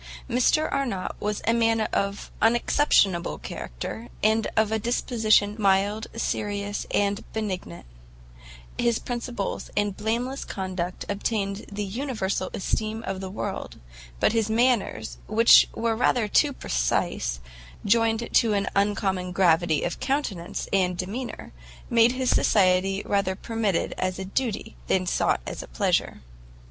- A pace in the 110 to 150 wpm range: Yes, slow, 135 wpm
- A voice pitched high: Yes, high, 205 Hz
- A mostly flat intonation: No, average, 3.3 semitones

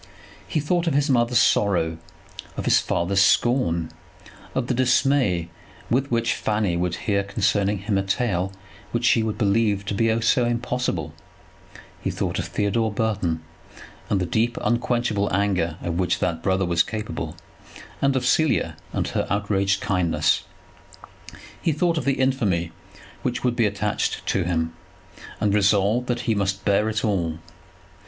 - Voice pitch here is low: Yes, low, 105 Hz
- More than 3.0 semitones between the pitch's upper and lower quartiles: Yes, average, 4.2 semitones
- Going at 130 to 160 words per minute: Yes, average, 155 wpm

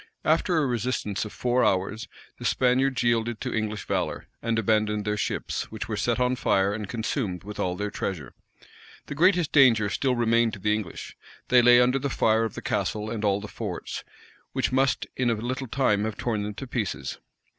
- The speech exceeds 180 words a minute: Yes, average, 200 wpm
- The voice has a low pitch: Yes, low, 115 Hz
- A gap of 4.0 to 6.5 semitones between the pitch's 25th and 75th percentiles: No, average, 3.1 semitones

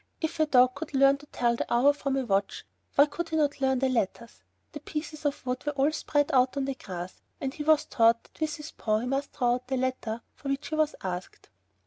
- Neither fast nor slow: No, fast, 250 wpm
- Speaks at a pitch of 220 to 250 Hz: No, very high, 270 Hz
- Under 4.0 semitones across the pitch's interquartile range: Yes, average, 3.2 semitones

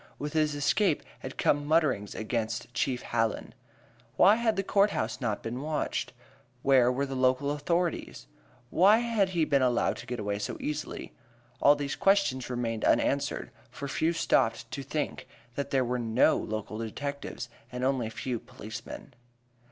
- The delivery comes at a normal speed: Yes, average, 165 wpm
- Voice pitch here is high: No, low, 135 Hz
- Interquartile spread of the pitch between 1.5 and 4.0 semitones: No, average, 4.5 semitones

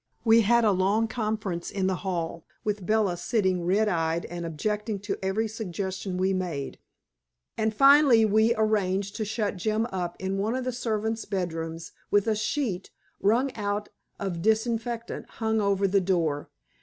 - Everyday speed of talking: Yes, average, 160 wpm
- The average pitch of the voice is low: No, high, 205 Hz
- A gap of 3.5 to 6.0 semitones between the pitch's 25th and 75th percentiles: No, average, 3.0 semitones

